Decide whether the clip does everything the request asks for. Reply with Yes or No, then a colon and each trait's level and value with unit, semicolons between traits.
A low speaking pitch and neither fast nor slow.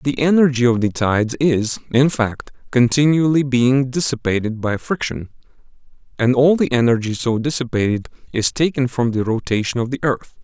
Yes: low, 125 Hz; average, 155 wpm